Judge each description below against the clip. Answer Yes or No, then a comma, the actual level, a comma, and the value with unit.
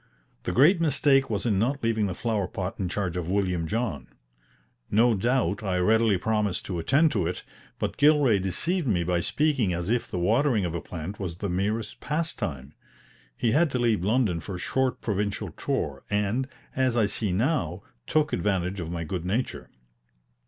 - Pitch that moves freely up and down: Yes, wide, 5.7 semitones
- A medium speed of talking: Yes, average, 180 wpm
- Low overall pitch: Yes, low, 105 Hz